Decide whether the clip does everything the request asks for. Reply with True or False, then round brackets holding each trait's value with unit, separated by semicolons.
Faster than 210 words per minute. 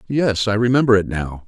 False (205 wpm)